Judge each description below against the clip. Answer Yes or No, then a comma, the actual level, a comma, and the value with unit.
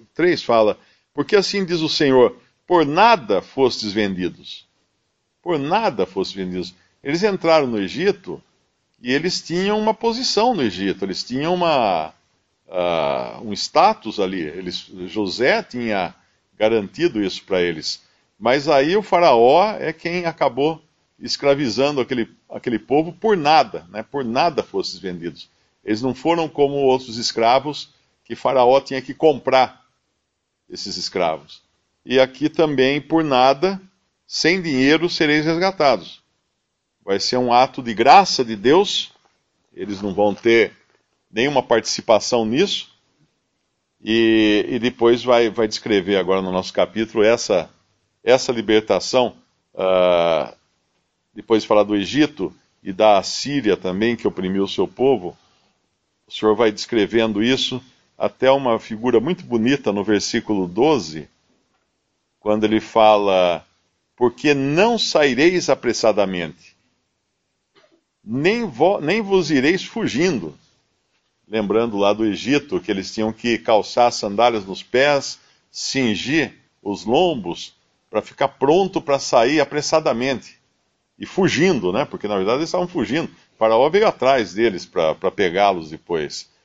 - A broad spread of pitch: Yes, wide, 6.4 semitones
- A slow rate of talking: No, average, 130 wpm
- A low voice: Yes, low, 120 Hz